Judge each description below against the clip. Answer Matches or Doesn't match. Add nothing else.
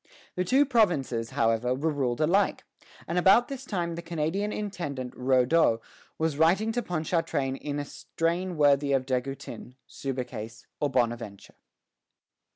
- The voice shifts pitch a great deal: Matches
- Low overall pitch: Doesn't match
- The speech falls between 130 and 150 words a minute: Matches